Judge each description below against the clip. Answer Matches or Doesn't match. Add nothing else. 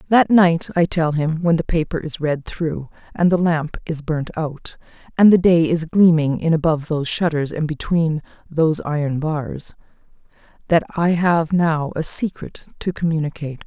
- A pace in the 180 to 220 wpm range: Doesn't match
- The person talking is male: Doesn't match